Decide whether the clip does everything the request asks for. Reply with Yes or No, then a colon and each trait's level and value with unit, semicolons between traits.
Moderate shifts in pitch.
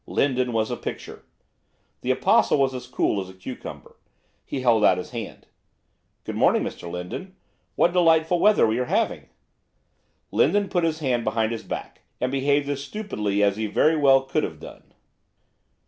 No: wide, 6.1 semitones